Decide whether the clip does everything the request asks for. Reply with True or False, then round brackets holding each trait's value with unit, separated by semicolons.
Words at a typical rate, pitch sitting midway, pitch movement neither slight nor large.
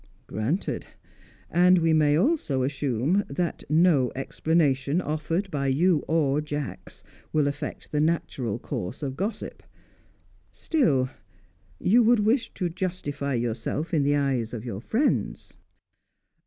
False (125 wpm; 150 Hz; 4.7 semitones)